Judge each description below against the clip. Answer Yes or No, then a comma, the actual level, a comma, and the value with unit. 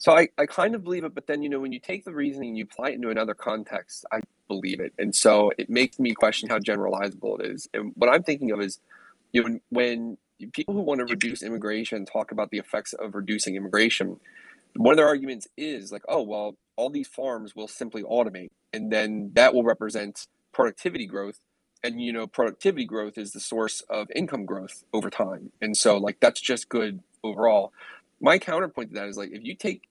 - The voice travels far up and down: No, average, 4.4 semitones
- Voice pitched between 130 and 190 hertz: No, low, 115 Hz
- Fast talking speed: Yes, fast, 220 wpm